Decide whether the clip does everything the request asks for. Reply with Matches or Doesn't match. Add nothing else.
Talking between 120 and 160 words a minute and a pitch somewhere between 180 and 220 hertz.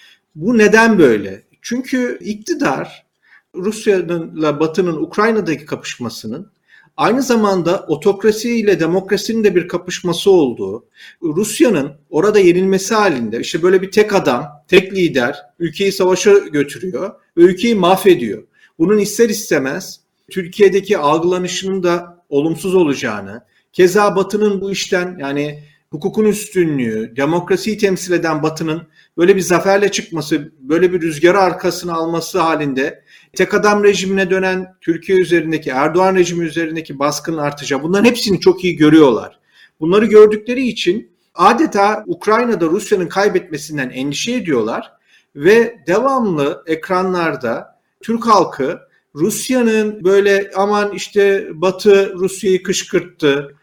Doesn't match